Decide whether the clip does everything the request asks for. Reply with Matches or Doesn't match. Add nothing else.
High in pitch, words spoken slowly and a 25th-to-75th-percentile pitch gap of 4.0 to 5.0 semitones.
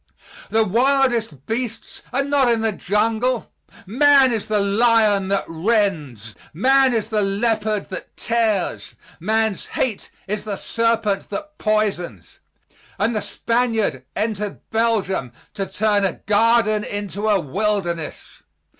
Doesn't match